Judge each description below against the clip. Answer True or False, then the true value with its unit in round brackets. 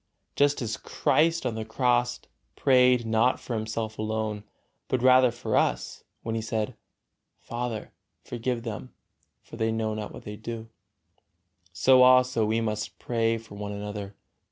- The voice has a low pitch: True (115 Hz)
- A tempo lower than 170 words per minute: True (150 wpm)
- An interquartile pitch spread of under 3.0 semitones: True (2.4 semitones)